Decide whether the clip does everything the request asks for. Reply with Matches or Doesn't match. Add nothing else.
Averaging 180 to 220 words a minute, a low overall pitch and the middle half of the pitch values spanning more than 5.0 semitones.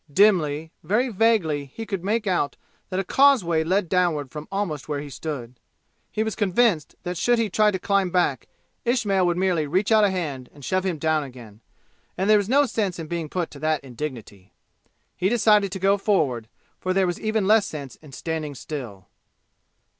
Doesn't match